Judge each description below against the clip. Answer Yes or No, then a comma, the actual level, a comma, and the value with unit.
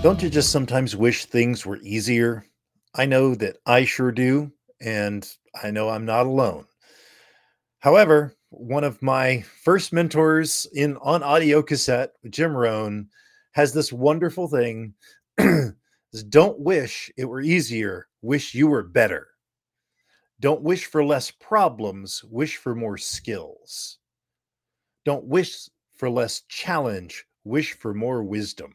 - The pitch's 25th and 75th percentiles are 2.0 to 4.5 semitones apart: No, average, 4.9 semitones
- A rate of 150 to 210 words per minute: No, slow, 135 wpm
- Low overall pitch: Yes, low, 130 Hz